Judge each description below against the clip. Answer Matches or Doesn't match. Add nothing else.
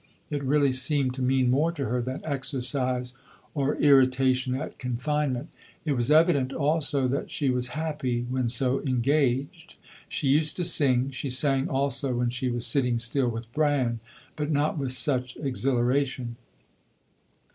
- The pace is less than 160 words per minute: Matches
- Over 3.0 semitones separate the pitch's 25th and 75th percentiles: Doesn't match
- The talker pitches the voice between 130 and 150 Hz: Matches